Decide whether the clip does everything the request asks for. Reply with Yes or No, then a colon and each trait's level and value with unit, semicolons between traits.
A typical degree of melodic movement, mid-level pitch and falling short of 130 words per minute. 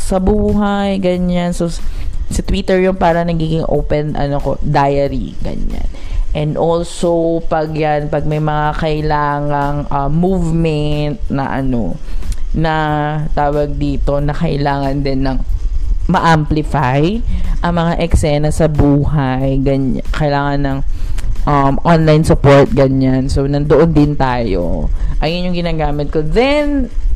Yes: average, 3.1 semitones; medium, 150 Hz; average, 120 wpm